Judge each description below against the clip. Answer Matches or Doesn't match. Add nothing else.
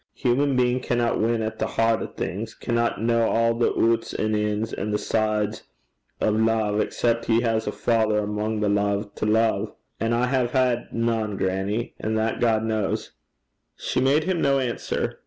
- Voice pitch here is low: Matches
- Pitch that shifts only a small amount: Matches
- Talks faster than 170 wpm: Matches